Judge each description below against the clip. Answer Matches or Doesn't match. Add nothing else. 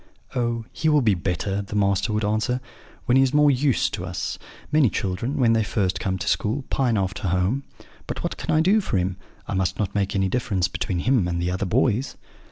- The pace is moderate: Doesn't match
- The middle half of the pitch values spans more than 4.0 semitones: Matches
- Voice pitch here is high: Doesn't match